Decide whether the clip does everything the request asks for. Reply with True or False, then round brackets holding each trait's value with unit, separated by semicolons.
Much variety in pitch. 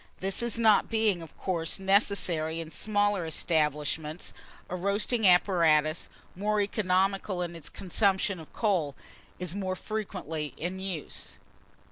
False (3.8 semitones)